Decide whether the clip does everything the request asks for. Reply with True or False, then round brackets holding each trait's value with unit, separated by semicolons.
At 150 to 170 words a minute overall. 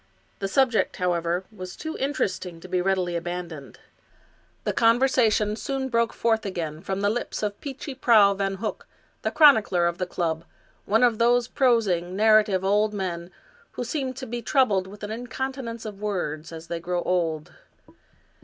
True (165 wpm)